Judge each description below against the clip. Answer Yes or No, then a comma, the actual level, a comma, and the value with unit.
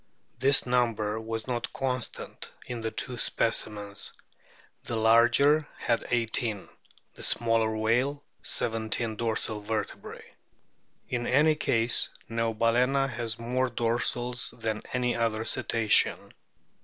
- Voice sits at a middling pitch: No, low, 115 Hz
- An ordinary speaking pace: No, slow, 105 wpm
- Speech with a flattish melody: Yes, narrow, 1.8 semitones